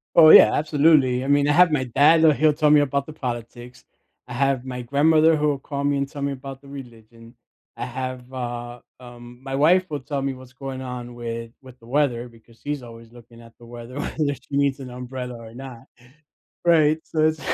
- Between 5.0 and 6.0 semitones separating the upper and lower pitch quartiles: No, average, 3.3 semitones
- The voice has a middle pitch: No, low, 130 Hz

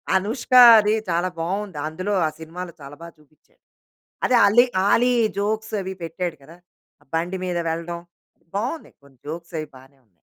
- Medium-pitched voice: Yes, medium, 175 Hz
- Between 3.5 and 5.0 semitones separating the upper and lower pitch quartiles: Yes, average, 4.4 semitones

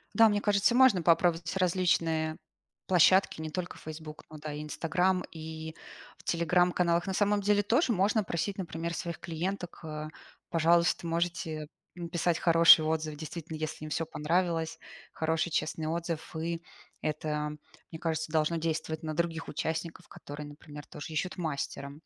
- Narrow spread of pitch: Yes, narrow, 2.1 semitones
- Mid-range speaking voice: Yes, medium, 165 Hz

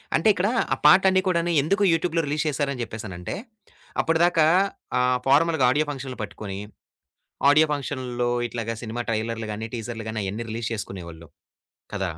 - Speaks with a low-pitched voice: Yes, low, 125 Hz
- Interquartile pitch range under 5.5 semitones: No, wide, 6.0 semitones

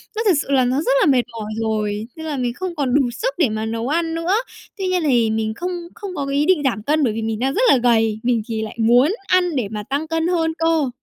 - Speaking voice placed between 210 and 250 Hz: No, very high, 270 Hz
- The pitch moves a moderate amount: No, wide, 6.5 semitones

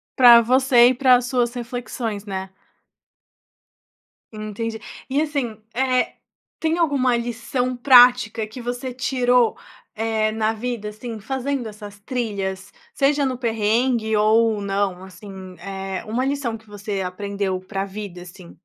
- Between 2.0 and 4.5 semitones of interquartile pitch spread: Yes, average, 3.5 semitones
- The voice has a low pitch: No, high, 225 Hz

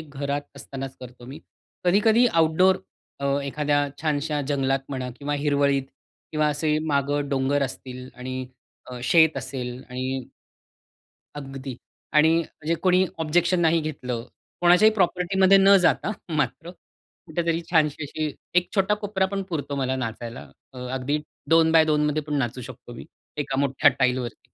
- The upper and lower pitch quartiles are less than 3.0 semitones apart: No, average, 3.7 semitones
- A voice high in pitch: No, medium, 145 Hz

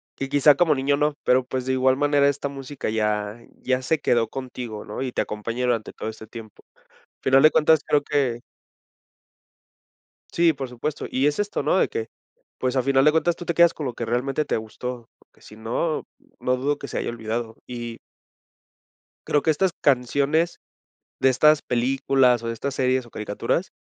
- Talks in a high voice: No, low, 130 Hz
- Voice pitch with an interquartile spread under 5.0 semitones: Yes, average, 3.6 semitones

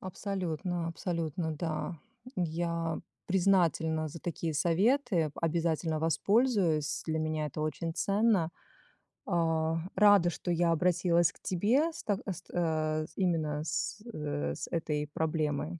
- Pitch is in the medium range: Yes, medium, 165 Hz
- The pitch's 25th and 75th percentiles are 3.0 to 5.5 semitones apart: No, narrow, 2.4 semitones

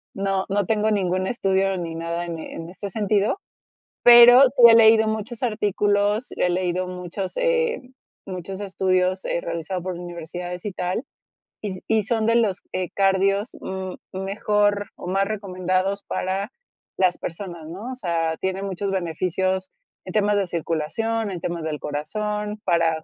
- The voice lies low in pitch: No, high, 190 Hz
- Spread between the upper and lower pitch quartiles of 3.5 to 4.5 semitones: No, average, 2.8 semitones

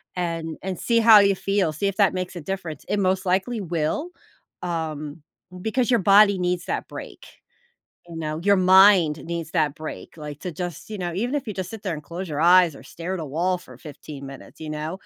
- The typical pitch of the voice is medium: Yes, medium, 180 Hz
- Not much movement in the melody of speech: No, average, 3.8 semitones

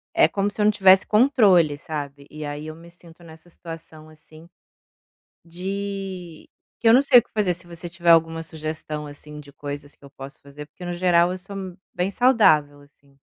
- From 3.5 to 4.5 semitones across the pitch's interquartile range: Yes, average, 3.8 semitones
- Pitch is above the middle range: No, medium, 165 Hz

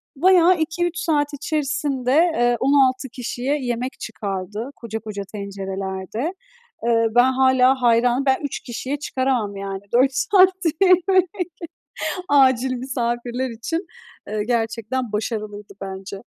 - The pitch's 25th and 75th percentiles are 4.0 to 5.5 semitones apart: Yes, average, 4.4 semitones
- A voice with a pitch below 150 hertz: No, very high, 250 Hz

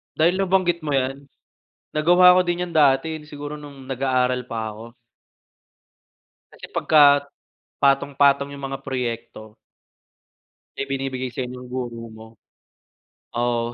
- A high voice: No, low, 135 Hz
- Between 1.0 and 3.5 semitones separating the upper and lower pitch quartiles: Yes, average, 3.1 semitones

